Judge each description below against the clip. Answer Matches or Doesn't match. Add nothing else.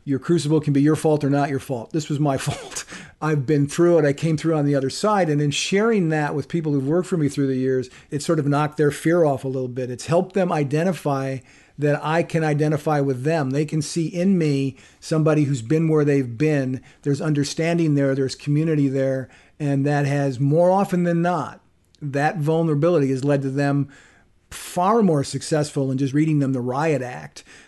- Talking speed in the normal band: Doesn't match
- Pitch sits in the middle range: Matches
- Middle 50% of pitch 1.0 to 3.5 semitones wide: Matches